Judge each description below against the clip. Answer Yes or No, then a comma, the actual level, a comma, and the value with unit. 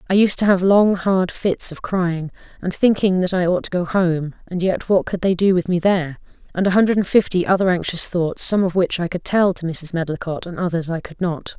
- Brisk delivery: Yes, fast, 240 wpm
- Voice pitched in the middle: Yes, medium, 180 Hz